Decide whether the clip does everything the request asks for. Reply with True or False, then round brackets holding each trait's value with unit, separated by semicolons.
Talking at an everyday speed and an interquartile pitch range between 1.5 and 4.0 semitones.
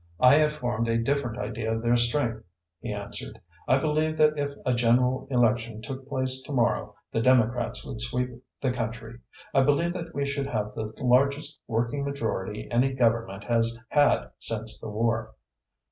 True (170 wpm; 3.4 semitones)